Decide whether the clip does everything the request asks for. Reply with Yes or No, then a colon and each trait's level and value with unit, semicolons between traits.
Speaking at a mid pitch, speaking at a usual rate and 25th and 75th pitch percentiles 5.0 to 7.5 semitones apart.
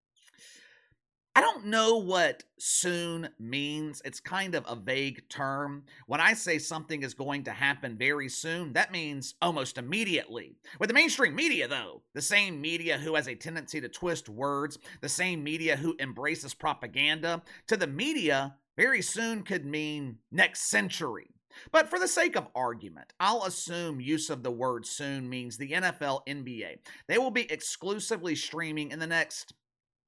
No: medium, 155 Hz; average, 160 wpm; average, 4.1 semitones